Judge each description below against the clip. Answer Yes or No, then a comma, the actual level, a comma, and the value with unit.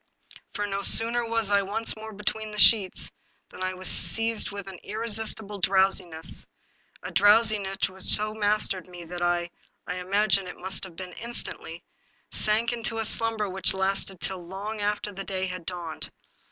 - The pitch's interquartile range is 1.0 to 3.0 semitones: Yes, narrow, 2.5 semitones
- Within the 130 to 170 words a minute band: Yes, average, 165 wpm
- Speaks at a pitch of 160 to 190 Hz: No, high, 200 Hz